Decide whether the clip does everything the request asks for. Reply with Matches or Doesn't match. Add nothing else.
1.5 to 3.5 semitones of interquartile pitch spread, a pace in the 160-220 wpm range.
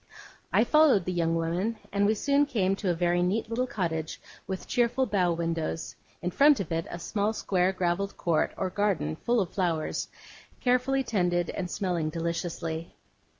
Doesn't match